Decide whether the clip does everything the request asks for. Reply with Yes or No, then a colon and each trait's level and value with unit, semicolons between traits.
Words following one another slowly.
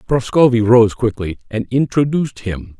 Yes: slow, 130 wpm